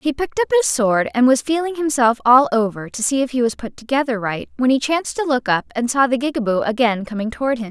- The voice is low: No, very high, 255 Hz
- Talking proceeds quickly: Yes, fast, 255 wpm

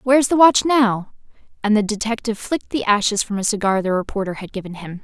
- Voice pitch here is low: No, high, 215 Hz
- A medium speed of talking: No, fast, 215 wpm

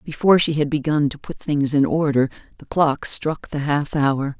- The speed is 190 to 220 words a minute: Yes, fast, 205 wpm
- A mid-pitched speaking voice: Yes, medium, 145 Hz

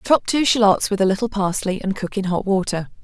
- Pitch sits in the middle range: No, high, 200 Hz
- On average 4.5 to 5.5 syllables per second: No, 5.7 syllables/s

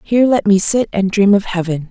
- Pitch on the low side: No, high, 205 Hz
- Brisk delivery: Yes, fast, 250 wpm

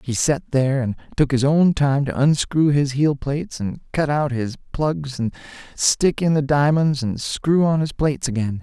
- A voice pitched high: No, medium, 140 Hz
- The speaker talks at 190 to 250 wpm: Yes, average, 195 wpm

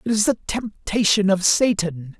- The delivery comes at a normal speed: Yes, average, 165 wpm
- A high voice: Yes, high, 200 Hz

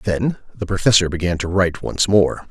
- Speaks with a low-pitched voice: Yes, very low, 95 Hz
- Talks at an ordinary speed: Yes, average, 190 wpm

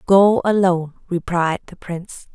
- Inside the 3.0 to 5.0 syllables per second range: Yes, 4.7 syllables/s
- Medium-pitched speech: Yes, medium, 180 Hz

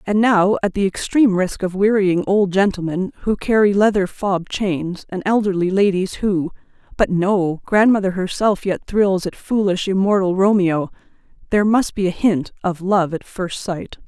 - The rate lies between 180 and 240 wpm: No, average, 160 wpm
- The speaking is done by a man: No, female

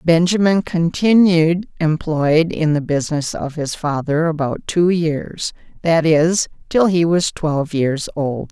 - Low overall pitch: No, medium, 165 Hz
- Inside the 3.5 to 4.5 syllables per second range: Yes, 3.9 syllables/s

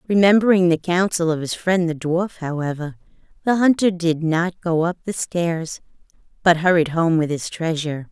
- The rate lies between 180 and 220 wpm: No, average, 170 wpm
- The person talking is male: No, female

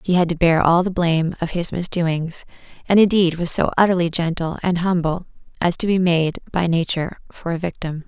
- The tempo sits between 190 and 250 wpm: Yes, average, 200 wpm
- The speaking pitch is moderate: Yes, medium, 170 Hz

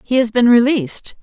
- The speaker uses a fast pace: No, average, 195 wpm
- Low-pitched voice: No, high, 235 Hz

